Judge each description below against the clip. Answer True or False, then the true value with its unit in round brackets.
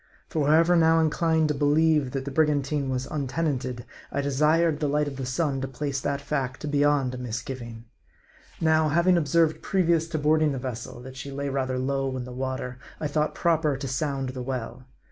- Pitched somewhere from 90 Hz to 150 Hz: True (140 Hz)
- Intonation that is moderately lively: True (3.0 semitones)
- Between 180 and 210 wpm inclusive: True (190 wpm)